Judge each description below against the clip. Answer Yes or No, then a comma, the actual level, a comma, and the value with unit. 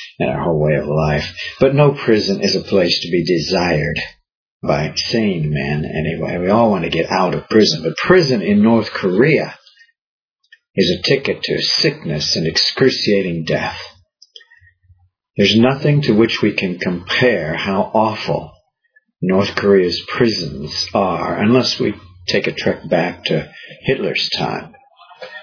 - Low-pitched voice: Yes, low, 115 Hz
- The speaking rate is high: No, average, 145 wpm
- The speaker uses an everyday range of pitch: No, wide, 8.7 semitones